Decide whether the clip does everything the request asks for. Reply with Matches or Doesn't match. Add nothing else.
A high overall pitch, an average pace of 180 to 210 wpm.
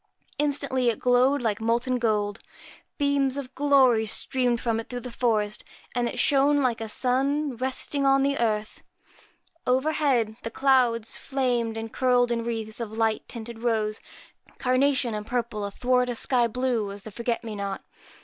Doesn't match